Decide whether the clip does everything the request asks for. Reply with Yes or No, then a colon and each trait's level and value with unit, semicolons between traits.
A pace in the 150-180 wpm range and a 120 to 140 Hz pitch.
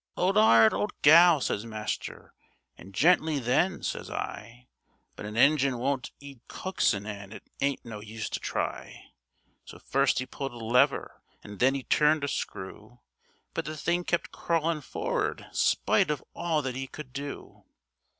Yes: average, 160 wpm; low, 135 Hz